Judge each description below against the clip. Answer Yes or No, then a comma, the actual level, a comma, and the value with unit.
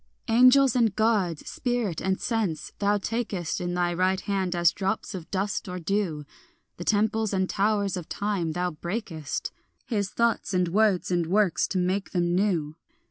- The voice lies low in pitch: No, high, 190 Hz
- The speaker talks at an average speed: Yes, average, 170 wpm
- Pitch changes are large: No, average, 3.2 semitones